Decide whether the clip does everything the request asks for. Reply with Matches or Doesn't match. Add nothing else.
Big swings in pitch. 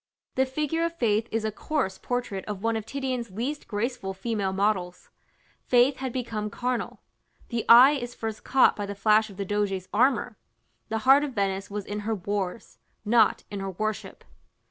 Doesn't match